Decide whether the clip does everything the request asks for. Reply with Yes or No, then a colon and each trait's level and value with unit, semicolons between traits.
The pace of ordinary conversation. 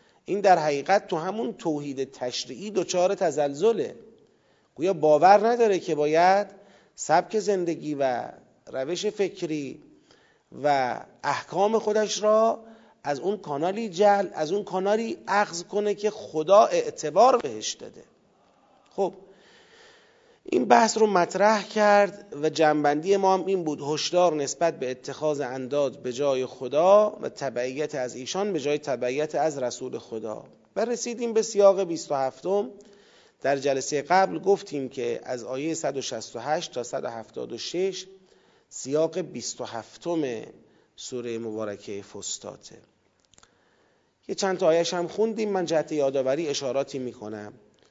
Yes: average, 125 wpm